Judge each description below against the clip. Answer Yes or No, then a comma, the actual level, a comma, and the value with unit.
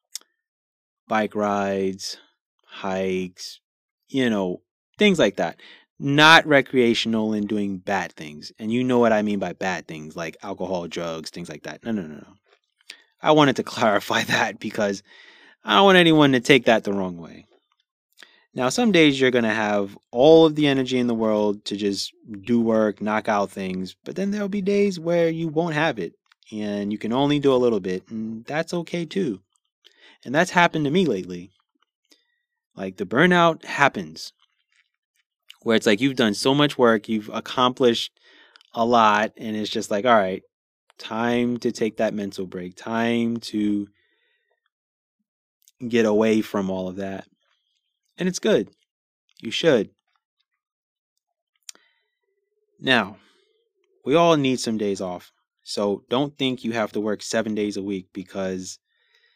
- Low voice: Yes, low, 115 Hz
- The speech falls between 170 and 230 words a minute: No, average, 160 wpm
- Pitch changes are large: Yes, wide, 8.5 semitones